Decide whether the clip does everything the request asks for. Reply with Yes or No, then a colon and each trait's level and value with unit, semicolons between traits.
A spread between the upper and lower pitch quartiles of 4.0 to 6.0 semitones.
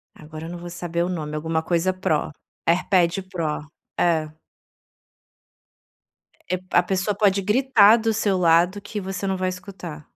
No: average, 3.0 semitones